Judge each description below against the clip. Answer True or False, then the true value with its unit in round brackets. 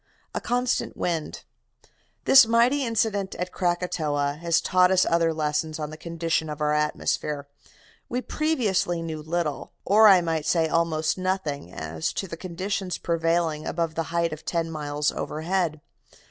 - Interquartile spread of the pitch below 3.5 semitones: True (3.1 semitones)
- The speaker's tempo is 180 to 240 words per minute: False (150 wpm)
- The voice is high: False (165 Hz)